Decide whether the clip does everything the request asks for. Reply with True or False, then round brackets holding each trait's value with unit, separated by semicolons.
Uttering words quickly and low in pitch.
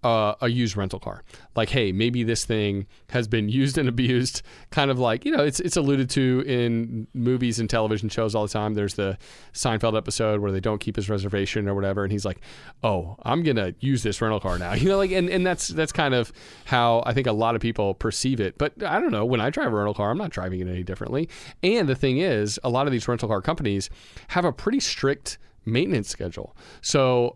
True (250 wpm; 115 Hz)